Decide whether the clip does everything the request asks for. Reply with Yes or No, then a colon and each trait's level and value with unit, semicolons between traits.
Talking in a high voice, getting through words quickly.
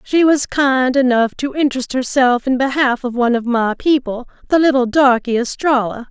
No: very high, 255 Hz; average, 175 wpm